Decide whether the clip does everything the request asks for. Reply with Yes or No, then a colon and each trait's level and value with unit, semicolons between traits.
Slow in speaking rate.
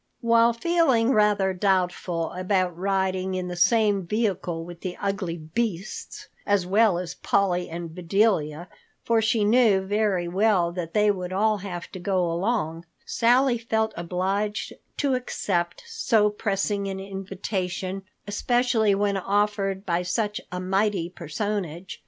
Yes: slow, 130 wpm